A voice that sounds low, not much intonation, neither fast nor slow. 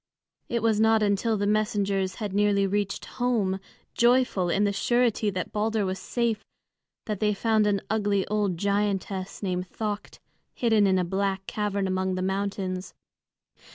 No: high, 205 Hz; narrow, 2.0 semitones; average, 155 wpm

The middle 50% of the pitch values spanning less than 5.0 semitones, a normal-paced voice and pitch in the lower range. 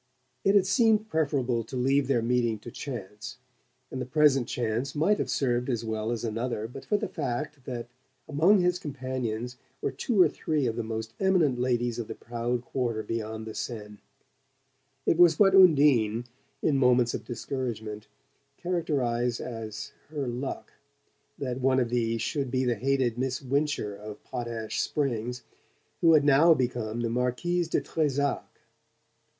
Yes: average, 4.0 semitones; average, 160 wpm; low, 125 Hz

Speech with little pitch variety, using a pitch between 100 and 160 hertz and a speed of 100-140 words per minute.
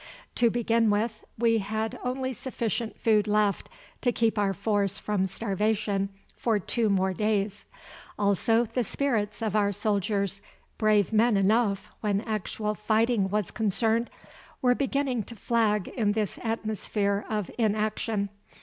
No: narrow, 2.1 semitones; high, 215 Hz; slow, 135 wpm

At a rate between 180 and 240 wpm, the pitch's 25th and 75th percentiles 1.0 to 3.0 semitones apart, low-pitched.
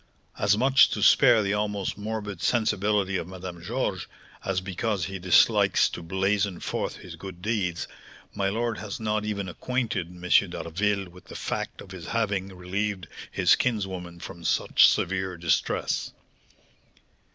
No: average, 145 wpm; average, 2.7 semitones; very low, 95 Hz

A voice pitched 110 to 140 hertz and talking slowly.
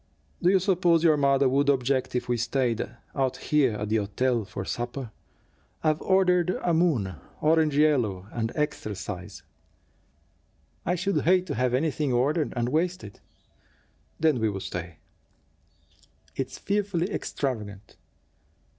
Yes: low, 135 Hz; slow, 130 wpm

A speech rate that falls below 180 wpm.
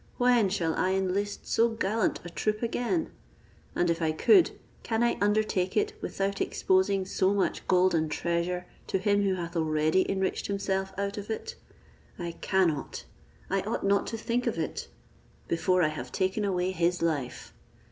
Yes: average, 165 wpm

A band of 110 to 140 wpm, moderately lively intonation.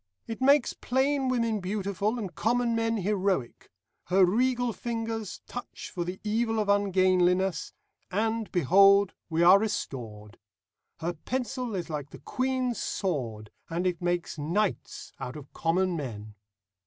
Yes: slow, 135 wpm; average, 4.8 semitones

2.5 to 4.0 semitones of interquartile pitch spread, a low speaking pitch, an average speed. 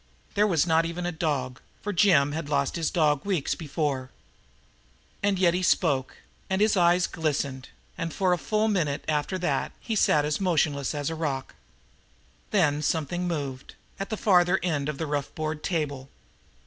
No: average, 3.7 semitones; medium, 160 Hz; average, 175 wpm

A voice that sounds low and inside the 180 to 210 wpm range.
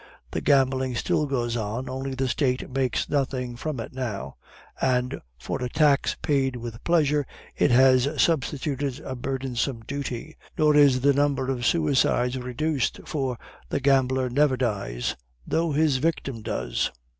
No: low, 130 Hz; average, 145 wpm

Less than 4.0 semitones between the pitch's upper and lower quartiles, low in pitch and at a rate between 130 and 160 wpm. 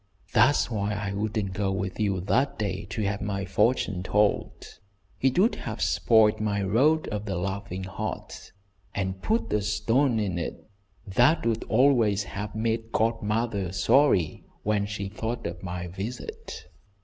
Yes: average, 2.8 semitones; low, 105 Hz; average, 150 wpm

